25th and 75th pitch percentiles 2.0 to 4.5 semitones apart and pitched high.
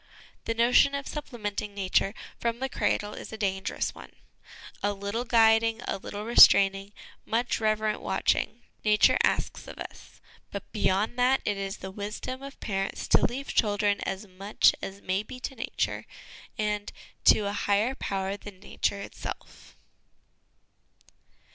Yes: average, 2.7 semitones; high, 210 Hz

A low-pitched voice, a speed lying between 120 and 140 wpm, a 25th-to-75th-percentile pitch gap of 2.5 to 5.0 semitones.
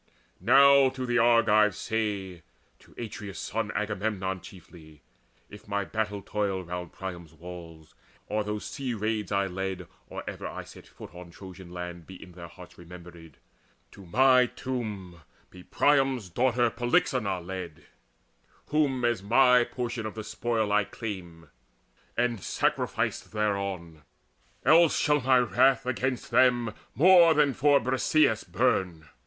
No: low, 105 Hz; slow, 135 wpm; wide, 5.4 semitones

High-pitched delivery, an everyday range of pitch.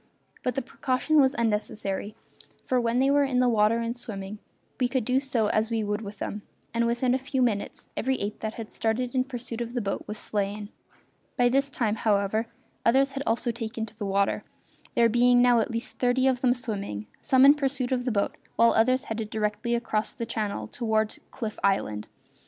Yes: high, 230 Hz; average, 3.0 semitones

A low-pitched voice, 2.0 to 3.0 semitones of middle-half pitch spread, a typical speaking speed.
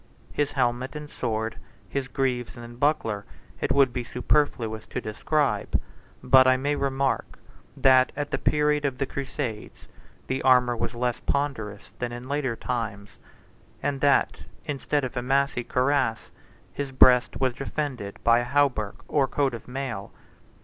Yes: low, 130 Hz; average, 2.7 semitones; average, 150 wpm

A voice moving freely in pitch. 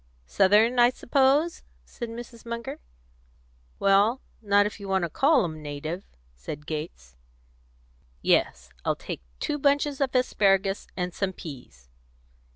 Yes: wide, 7.4 semitones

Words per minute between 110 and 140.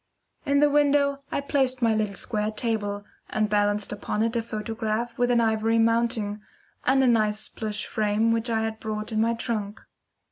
No: average, 180 wpm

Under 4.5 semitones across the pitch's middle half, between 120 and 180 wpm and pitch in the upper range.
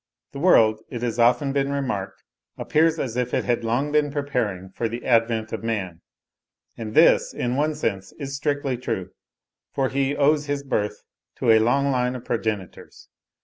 No: average, 3.9 semitones; average, 175 wpm; low, 125 Hz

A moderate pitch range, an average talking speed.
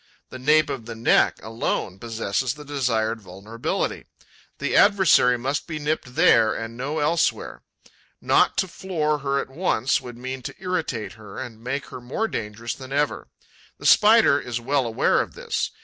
Yes: average, 4.5 semitones; average, 165 wpm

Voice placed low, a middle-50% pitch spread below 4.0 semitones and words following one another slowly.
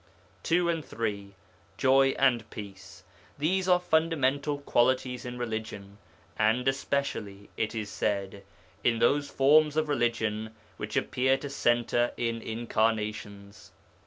No: low, 120 Hz; average, 4.6 semitones; slow, 120 wpm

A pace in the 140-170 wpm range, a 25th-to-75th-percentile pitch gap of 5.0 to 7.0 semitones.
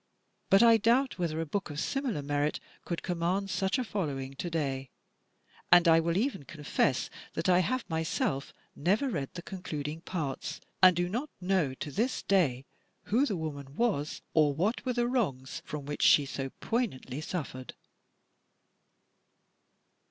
Yes: average, 155 wpm; wide, 5.5 semitones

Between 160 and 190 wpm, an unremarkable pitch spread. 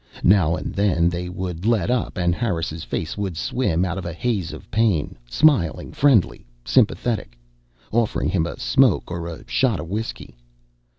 Yes: average, 165 wpm; average, 4.9 semitones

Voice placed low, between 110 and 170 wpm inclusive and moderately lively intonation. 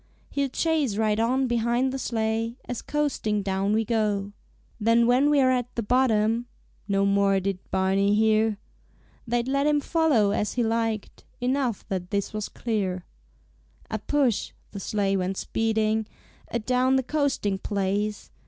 No: high, 220 Hz; average, 150 wpm; average, 3.8 semitones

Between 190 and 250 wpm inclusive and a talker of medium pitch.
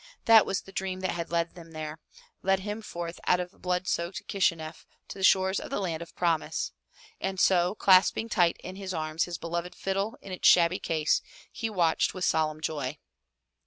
Yes: average, 200 wpm; medium, 180 Hz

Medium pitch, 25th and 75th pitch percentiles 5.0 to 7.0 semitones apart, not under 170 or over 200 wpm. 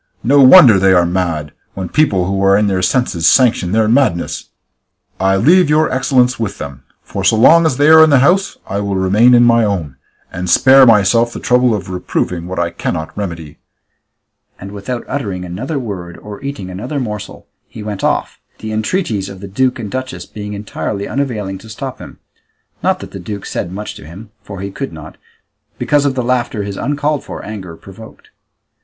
No: low, 105 Hz; average, 5.3 semitones; average, 195 wpm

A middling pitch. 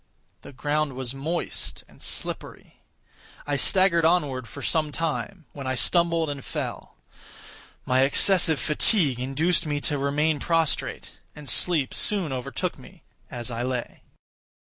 Yes: medium, 150 Hz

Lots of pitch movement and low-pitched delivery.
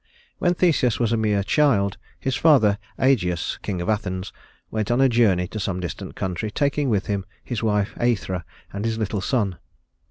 No: average, 4.0 semitones; low, 105 Hz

